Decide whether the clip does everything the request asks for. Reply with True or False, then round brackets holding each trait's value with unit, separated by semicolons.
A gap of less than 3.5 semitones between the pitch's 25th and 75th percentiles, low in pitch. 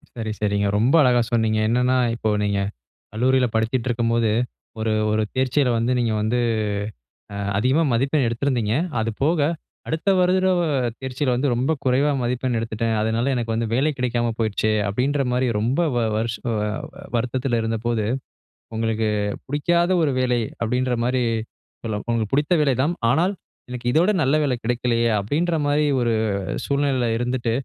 True (3.0 semitones; 125 Hz)